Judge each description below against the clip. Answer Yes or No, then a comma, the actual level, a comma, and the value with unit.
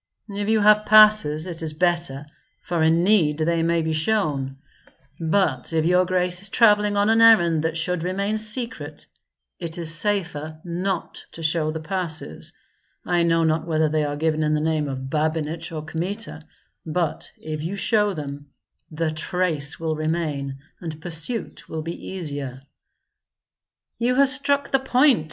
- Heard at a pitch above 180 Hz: No, medium, 165 Hz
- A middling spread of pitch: Yes, average, 4.1 semitones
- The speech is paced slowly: No, average, 160 wpm